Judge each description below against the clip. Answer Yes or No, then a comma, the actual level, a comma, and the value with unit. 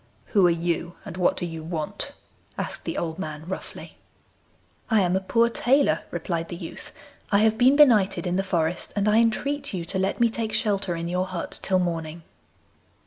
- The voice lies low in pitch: No, medium, 185 Hz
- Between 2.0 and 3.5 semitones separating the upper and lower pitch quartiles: No, average, 4.2 semitones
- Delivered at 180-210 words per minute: Yes, average, 195 wpm